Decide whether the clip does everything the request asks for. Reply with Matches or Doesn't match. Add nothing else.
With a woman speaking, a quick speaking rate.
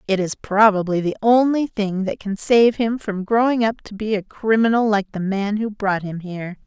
Matches